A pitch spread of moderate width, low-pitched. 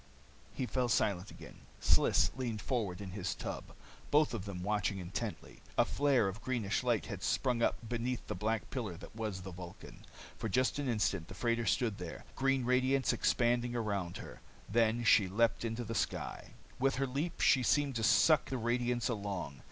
Yes: average, 4.0 semitones; low, 115 Hz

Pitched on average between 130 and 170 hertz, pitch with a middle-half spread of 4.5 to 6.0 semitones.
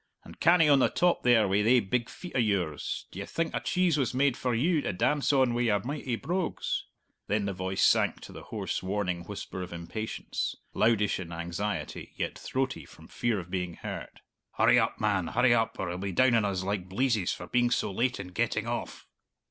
No: low, 110 Hz; average, 5.2 semitones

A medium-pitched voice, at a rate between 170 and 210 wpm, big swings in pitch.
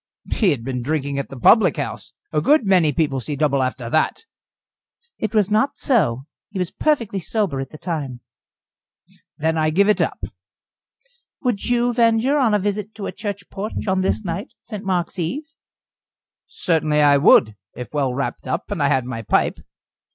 Yes: medium, 175 Hz; average, 180 wpm; wide, 7.1 semitones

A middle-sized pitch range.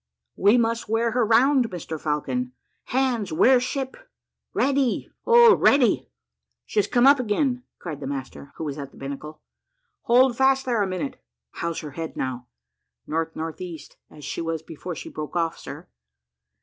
No: wide, 8.1 semitones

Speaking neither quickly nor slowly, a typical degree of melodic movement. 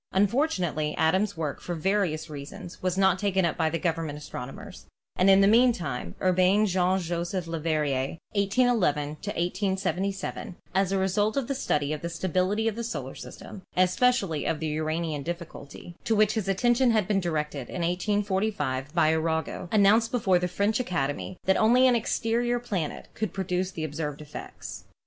Yes: average, 165 wpm; average, 4.4 semitones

